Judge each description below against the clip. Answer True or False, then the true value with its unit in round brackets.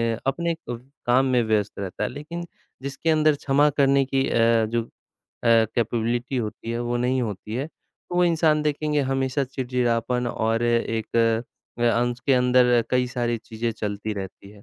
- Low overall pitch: True (120 Hz)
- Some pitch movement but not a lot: True (3.0 semitones)